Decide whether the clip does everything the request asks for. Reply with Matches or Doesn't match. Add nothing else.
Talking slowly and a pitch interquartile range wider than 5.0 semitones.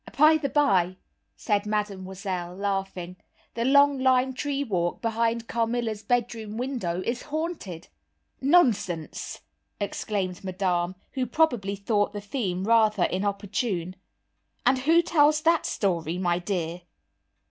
Matches